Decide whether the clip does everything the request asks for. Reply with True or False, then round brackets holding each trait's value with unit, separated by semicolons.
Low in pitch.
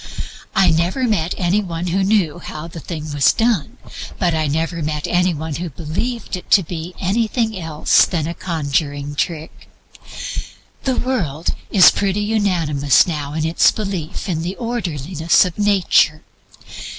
False (170 Hz)